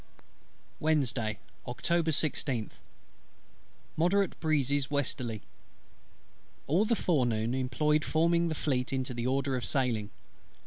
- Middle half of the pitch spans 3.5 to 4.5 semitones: Yes, average, 4.2 semitones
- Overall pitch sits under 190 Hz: Yes, medium, 140 Hz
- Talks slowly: Yes, slow, 100 wpm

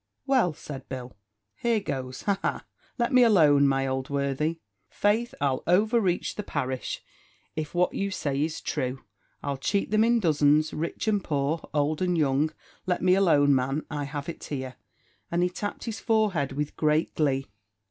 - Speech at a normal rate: Yes, average, 170 wpm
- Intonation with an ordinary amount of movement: No, wide, 5.7 semitones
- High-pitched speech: No, medium, 155 Hz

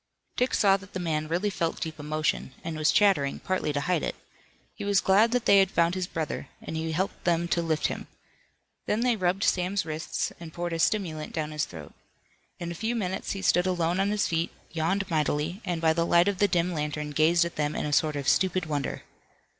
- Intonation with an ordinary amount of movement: Yes, average, 3.5 semitones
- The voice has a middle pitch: Yes, medium, 170 Hz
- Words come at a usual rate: No, fast, 225 wpm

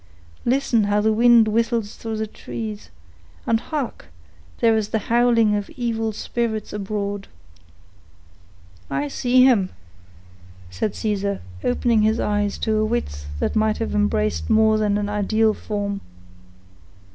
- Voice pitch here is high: Yes, high, 215 Hz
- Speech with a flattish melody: Yes, narrow, 1.9 semitones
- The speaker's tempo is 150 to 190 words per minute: No, slow, 135 wpm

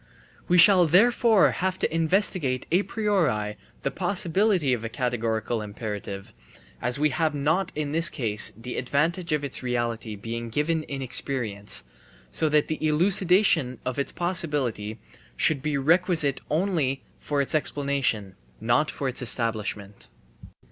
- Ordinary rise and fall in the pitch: No, wide, 6.0 semitones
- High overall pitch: No, medium, 140 Hz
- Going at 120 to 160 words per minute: Yes, average, 140 wpm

